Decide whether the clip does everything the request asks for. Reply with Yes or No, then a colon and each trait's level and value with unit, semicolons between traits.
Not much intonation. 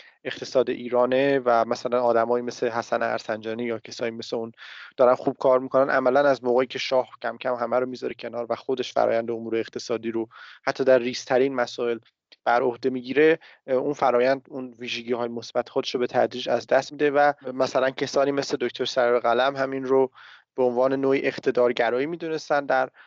Yes: narrow, 2.0 semitones